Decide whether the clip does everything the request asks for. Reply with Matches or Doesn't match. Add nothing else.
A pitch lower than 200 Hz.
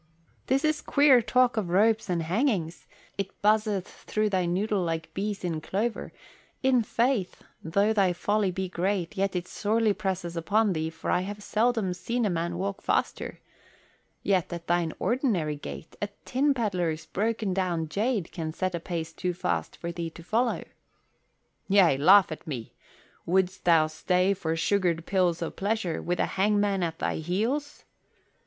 Matches